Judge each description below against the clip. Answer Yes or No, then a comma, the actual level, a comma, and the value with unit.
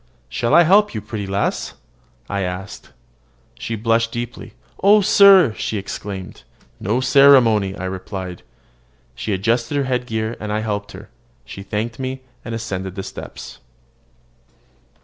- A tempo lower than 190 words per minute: Yes, average, 140 wpm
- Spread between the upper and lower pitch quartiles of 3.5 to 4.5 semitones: Yes, average, 4.1 semitones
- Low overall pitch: Yes, low, 110 Hz